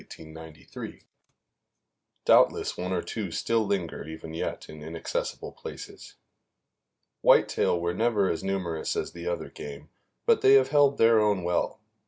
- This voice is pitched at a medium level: No, very low, 90 Hz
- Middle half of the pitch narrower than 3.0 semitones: No, average, 5.0 semitones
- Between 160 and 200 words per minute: No, slow, 135 wpm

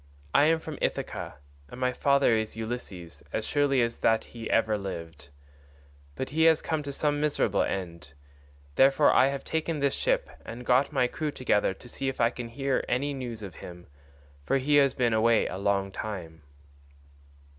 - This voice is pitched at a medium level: No, low, 125 Hz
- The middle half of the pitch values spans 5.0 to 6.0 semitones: Yes, wide, 5.4 semitones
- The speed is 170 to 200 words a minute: Yes, average, 180 wpm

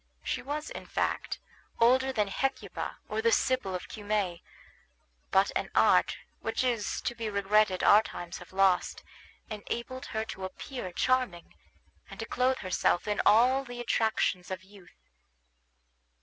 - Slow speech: No, average, 150 wpm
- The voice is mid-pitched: No, high, 215 Hz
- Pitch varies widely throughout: No, average, 4.6 semitones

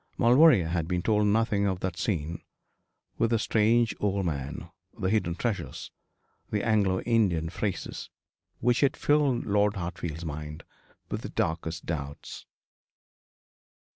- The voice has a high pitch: No, very low, 95 Hz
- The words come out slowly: Yes, slow, 130 wpm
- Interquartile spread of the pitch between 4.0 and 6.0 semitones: Yes, average, 4.9 semitones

